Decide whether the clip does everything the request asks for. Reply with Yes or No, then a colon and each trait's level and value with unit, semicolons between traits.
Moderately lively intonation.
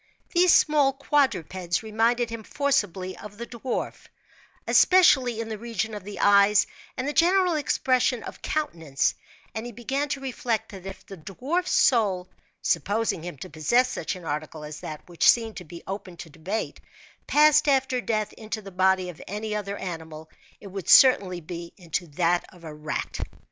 No: wide, 6.1 semitones